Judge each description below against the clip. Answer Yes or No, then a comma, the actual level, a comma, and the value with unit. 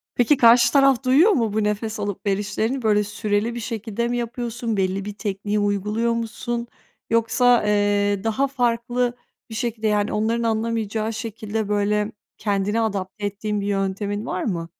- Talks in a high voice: Yes, high, 220 Hz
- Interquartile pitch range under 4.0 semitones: Yes, narrow, 2.4 semitones